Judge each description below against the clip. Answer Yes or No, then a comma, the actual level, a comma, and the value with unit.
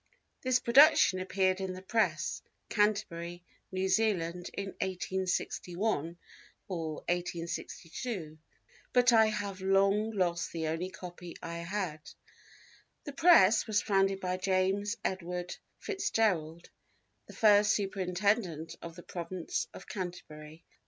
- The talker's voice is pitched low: No, medium, 185 Hz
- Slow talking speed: Yes, slow, 110 wpm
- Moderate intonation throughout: Yes, average, 3.1 semitones